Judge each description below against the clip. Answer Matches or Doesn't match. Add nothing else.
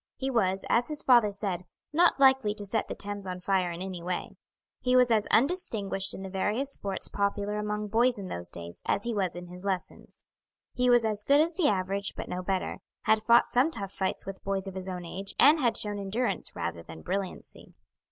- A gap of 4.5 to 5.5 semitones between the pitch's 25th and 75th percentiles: Doesn't match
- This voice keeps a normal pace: Doesn't match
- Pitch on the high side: Matches